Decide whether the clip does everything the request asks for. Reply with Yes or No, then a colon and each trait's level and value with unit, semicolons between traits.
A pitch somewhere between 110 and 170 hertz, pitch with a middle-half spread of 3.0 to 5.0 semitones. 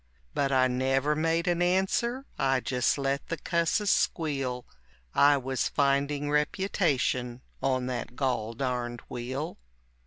Yes: low, 135 Hz; average, 3.9 semitones